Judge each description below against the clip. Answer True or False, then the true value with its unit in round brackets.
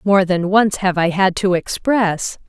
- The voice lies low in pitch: False (190 Hz)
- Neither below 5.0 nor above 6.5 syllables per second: False (3.9 syllables/s)